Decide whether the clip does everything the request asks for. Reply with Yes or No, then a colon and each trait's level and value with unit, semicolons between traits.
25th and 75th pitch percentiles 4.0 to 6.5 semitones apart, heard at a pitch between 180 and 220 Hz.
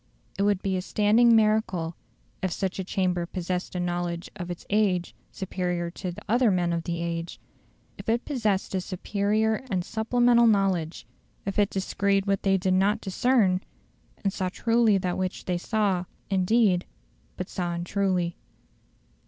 No: average, 3.0 semitones; high, 190 Hz